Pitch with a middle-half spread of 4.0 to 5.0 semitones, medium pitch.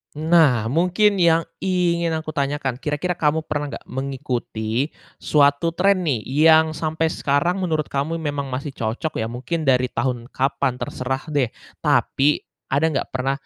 No: average, 3.6 semitones; medium, 145 Hz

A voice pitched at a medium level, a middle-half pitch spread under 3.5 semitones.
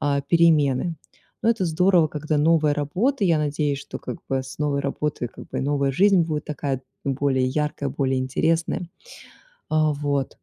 Yes: medium, 150 Hz; average, 2.8 semitones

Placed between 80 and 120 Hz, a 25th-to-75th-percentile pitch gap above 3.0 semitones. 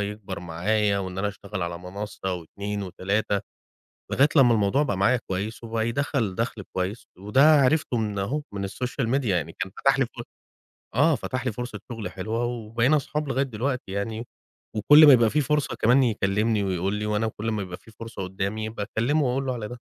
Yes: low, 110 Hz; average, 4.0 semitones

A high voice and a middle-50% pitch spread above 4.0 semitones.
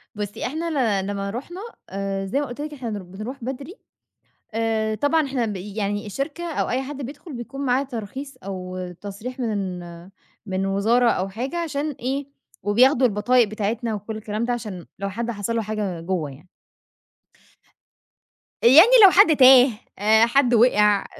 Yes: high, 230 Hz; average, 4.7 semitones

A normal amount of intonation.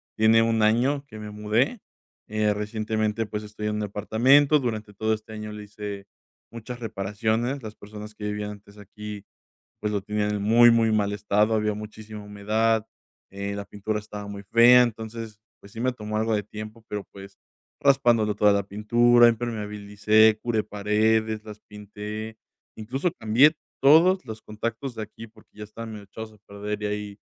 No: narrow, 1.4 semitones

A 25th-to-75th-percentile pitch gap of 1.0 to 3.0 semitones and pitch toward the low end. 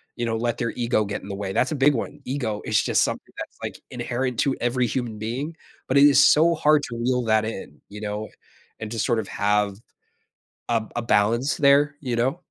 No: average, 3.7 semitones; low, 120 Hz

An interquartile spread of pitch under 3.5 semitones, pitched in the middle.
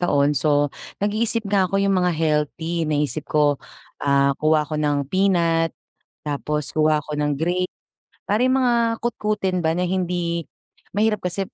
No: average, 4.1 semitones; medium, 165 Hz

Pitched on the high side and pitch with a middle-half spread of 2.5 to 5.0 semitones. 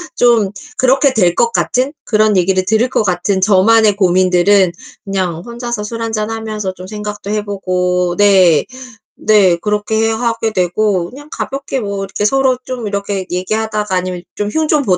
Yes: high, 210 Hz; average, 3.2 semitones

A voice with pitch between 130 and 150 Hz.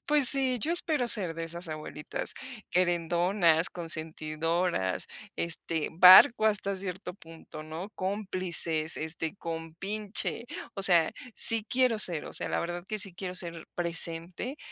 No: medium, 175 Hz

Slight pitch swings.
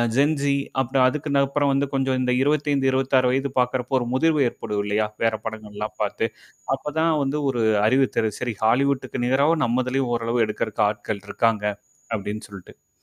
No: average, 3.7 semitones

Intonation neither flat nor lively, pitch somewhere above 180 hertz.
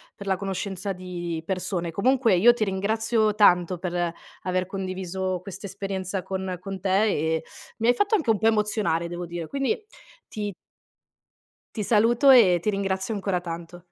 Yes: average, 3.0 semitones; high, 190 Hz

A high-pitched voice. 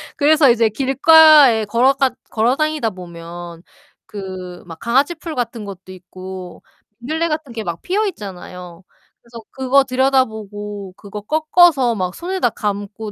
Yes: high, 230 Hz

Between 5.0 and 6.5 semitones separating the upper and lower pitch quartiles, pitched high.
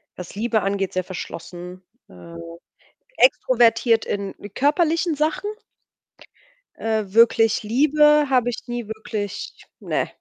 Yes: wide, 5.5 semitones; high, 225 Hz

